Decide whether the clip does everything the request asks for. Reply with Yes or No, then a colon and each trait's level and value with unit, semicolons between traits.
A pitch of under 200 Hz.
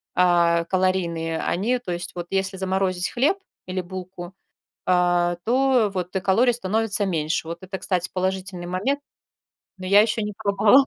Yes: medium, 185 Hz